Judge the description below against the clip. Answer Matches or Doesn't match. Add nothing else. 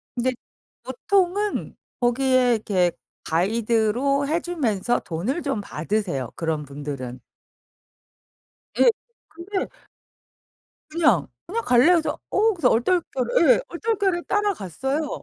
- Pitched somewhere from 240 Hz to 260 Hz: Matches